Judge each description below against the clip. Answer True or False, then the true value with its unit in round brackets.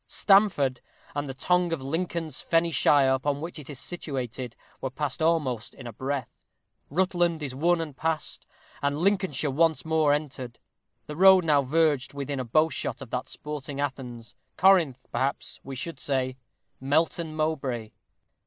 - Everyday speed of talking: True (155 wpm)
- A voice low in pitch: False (145 Hz)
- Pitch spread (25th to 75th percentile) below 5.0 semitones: True (3.7 semitones)